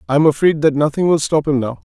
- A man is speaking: Yes, male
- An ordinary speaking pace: No, fast, 280 wpm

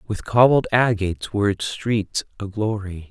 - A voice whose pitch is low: Yes, low, 105 Hz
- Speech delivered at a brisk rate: No, average, 155 wpm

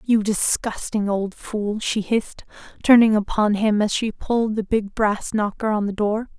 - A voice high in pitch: Yes, high, 215 Hz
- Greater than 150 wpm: Yes, average, 180 wpm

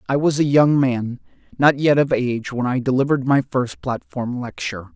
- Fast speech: No, average, 195 wpm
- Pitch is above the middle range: No, low, 130 Hz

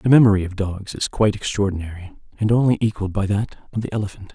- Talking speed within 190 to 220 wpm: Yes, fast, 205 wpm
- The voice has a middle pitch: No, low, 100 Hz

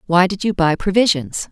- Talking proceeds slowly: No, average, 200 wpm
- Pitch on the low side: No, medium, 185 Hz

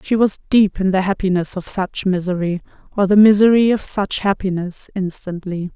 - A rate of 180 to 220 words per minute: No, average, 165 wpm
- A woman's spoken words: Yes, female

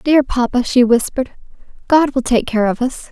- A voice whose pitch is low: No, very high, 250 Hz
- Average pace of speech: Yes, average, 190 wpm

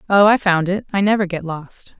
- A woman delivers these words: Yes, female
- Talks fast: Yes, fast, 240 wpm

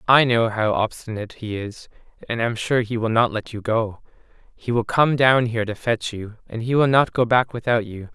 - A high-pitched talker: No, low, 115 Hz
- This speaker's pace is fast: Yes, fast, 230 wpm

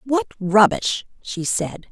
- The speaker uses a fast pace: No, slow, 125 wpm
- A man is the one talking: No, female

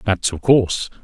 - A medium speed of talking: Yes, average, 175 wpm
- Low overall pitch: Yes, low, 100 Hz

